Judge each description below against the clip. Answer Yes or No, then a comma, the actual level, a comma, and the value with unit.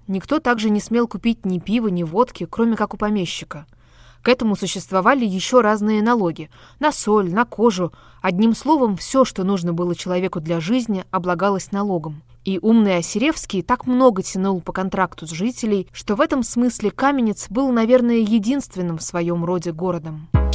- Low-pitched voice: No, high, 200 Hz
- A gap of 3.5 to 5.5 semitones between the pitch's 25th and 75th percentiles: Yes, average, 4.8 semitones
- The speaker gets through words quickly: Yes, fast, 165 wpm